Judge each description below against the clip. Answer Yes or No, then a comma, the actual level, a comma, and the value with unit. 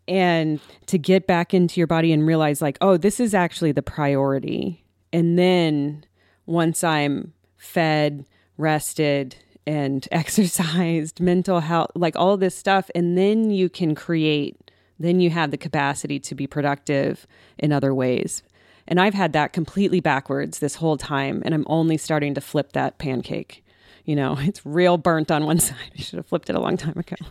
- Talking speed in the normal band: Yes, average, 175 wpm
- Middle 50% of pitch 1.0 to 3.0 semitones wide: No, average, 3.4 semitones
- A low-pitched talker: No, medium, 160 Hz